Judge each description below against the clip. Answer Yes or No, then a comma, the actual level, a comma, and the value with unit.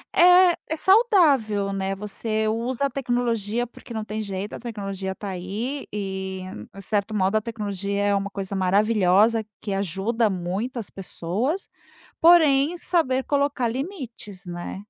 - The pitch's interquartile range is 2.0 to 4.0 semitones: No, average, 4.7 semitones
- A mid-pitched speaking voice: No, high, 215 Hz